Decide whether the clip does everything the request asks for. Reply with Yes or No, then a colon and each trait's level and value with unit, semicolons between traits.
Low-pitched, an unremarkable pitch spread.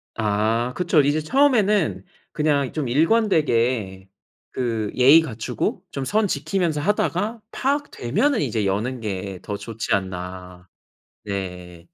No: low, 125 Hz; wide, 8.6 semitones